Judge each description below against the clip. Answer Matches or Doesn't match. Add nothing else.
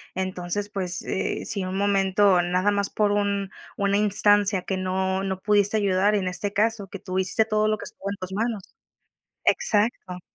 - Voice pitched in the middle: Doesn't match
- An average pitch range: Doesn't match